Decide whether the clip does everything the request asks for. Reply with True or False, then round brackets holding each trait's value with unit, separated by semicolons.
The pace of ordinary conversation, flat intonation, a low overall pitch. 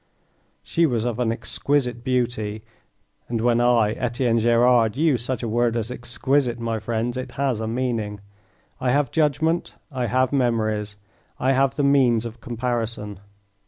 True (155 wpm; 2.2 semitones; 120 Hz)